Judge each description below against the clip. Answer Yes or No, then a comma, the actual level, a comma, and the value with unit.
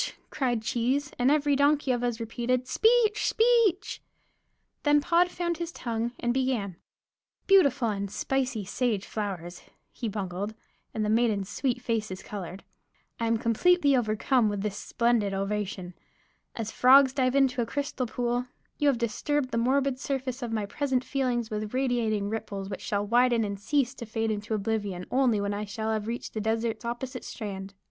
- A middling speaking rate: Yes, average, 165 wpm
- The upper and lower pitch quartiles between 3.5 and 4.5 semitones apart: Yes, average, 4.1 semitones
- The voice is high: Yes, high, 235 Hz